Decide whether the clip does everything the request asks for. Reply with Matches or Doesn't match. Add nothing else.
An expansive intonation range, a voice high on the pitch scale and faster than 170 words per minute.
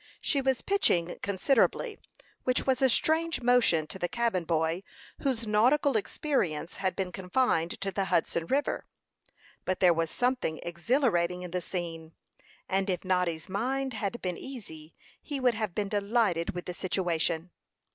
Doesn't match